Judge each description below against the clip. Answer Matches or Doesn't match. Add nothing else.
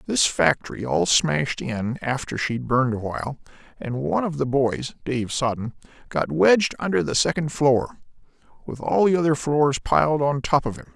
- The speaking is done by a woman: Doesn't match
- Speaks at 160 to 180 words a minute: Matches